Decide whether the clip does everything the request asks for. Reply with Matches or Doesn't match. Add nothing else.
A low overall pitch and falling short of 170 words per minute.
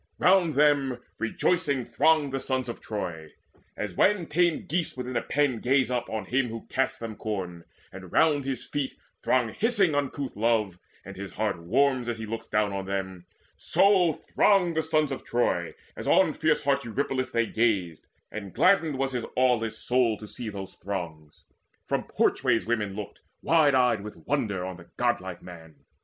Doesn't match